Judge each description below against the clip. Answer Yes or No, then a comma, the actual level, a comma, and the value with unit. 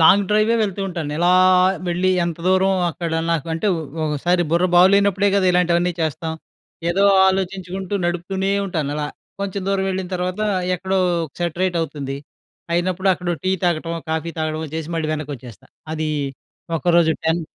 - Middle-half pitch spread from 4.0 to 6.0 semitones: No, average, 2.7 semitones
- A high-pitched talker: No, medium, 175 Hz